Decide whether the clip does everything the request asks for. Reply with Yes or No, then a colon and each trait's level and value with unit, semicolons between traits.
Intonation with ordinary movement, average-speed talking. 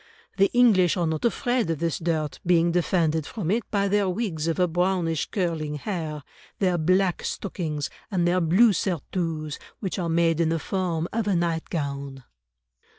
Yes: average, 3.0 semitones; average, 165 wpm